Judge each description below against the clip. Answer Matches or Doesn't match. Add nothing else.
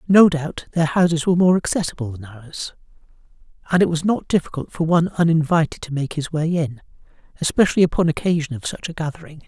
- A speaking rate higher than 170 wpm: Matches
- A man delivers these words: Matches